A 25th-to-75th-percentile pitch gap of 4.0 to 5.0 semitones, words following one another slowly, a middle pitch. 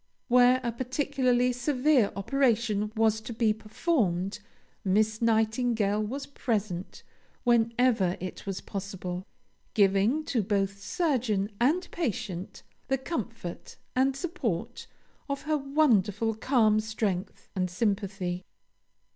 No: average, 4.3 semitones; slow, 105 wpm; high, 220 Hz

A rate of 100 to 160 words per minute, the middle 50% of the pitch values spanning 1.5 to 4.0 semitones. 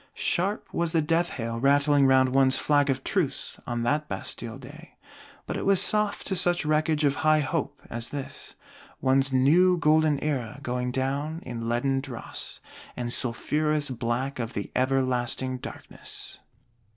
Yes: average, 150 wpm; average, 3.3 semitones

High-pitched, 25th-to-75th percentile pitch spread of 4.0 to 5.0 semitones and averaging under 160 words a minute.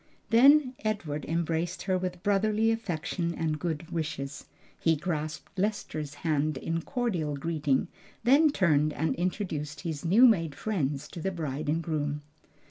No: medium, 165 Hz; average, 4.6 semitones; average, 140 wpm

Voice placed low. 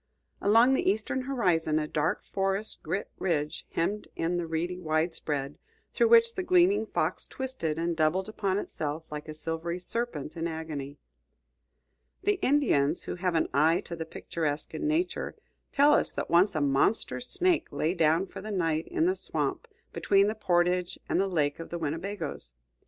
No: medium, 175 Hz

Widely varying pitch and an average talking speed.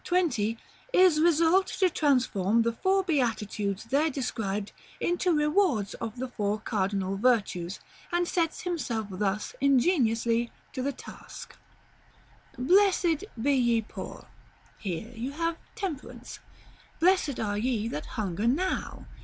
No: wide, 7.7 semitones; slow, 120 wpm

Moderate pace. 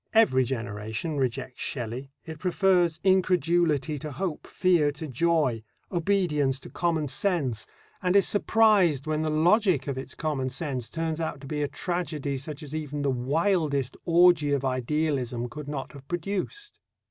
Yes: average, 155 wpm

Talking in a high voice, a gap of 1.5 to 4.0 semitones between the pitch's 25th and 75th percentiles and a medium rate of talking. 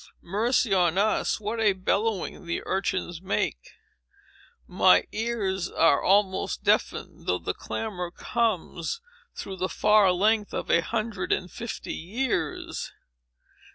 No: high, 195 Hz; average, 3.5 semitones; slow, 120 wpm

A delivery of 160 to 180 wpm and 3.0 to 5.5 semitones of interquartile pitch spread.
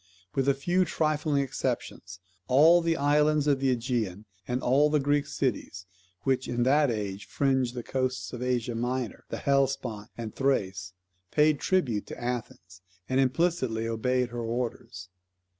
No: average, 150 wpm; average, 3.7 semitones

